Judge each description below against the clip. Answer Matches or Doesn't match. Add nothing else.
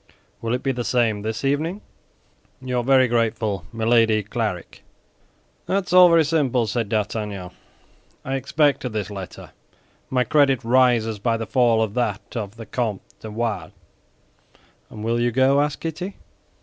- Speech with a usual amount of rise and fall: Matches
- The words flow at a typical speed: Matches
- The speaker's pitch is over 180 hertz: Doesn't match